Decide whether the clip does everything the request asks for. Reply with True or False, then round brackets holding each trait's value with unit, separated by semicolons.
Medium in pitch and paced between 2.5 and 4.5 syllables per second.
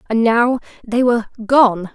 False (230 Hz; 4.4 syllables/s)